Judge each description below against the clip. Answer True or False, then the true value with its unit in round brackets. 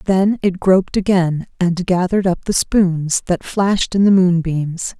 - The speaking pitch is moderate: True (180 Hz)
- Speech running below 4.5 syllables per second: True (4.3 syllables/s)